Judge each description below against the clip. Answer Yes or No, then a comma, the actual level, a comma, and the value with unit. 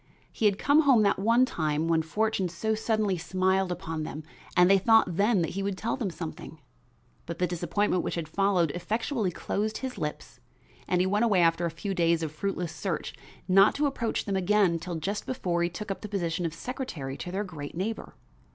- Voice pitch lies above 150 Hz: Yes, high, 190 Hz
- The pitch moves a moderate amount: Yes, average, 4.0 semitones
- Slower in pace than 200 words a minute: No, fast, 205 wpm